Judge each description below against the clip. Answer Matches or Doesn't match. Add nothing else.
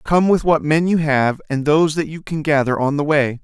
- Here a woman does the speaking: Doesn't match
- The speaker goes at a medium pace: Doesn't match